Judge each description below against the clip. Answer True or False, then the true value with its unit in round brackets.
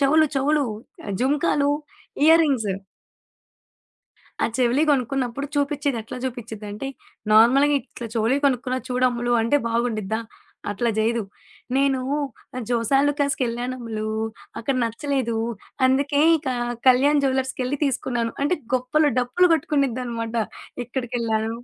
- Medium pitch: False (255 Hz)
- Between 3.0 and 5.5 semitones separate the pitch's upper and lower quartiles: True (3.3 semitones)